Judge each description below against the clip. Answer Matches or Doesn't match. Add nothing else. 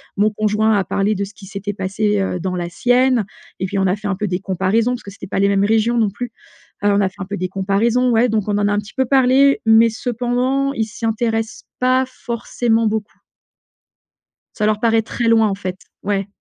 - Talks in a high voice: Matches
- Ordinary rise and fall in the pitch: Matches